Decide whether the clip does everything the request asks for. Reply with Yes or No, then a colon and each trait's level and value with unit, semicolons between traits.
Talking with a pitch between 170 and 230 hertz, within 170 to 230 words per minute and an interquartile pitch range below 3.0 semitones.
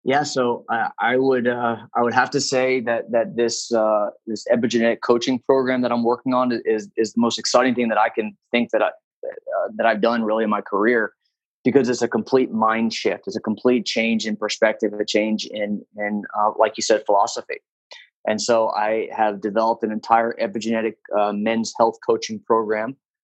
No: low, 115 Hz; average, 200 wpm; narrow, 2.6 semitones